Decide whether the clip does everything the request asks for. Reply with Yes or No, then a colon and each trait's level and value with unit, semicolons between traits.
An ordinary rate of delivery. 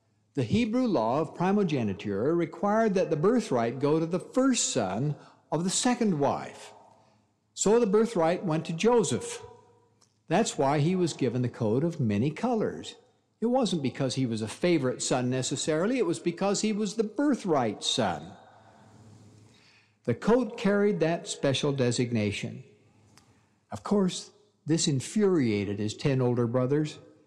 Yes: average, 145 wpm